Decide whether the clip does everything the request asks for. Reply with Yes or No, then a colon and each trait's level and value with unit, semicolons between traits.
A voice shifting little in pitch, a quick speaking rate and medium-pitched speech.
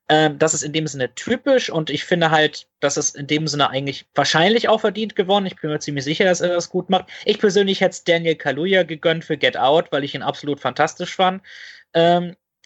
No: average, 3.7 semitones; fast, 230 wpm; medium, 165 Hz